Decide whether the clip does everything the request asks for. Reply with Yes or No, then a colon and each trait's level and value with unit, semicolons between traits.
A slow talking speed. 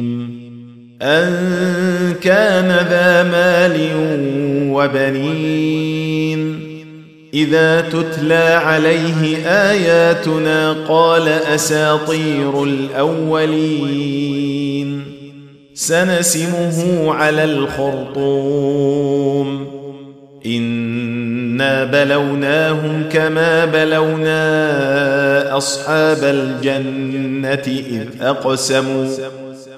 Yes: slow, 45 wpm